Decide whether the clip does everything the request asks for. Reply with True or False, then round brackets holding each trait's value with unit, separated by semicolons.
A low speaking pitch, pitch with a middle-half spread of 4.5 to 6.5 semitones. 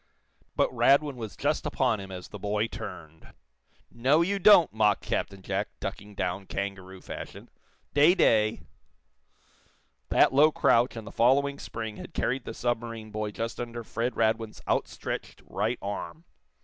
False (115 Hz; 3.8 semitones)